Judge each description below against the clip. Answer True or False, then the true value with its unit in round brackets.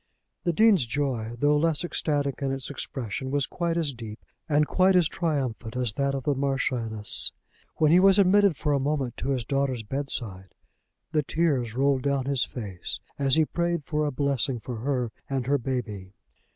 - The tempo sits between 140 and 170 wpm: False (180 wpm)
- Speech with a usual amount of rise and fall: True (3.5 semitones)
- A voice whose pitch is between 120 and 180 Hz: True (140 Hz)